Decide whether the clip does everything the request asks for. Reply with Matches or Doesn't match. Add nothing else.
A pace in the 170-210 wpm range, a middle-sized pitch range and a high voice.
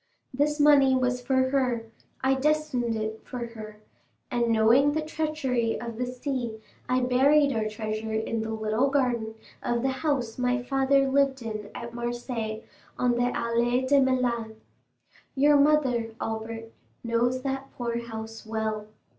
Doesn't match